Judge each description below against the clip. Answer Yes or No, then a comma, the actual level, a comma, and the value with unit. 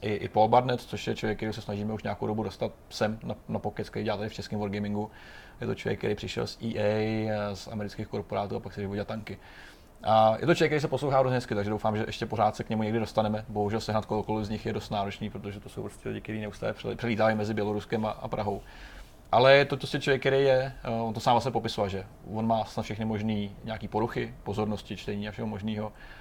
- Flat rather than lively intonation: Yes, narrow, 1.6 semitones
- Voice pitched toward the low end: Yes, low, 110 Hz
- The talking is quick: Yes, fast, 230 wpm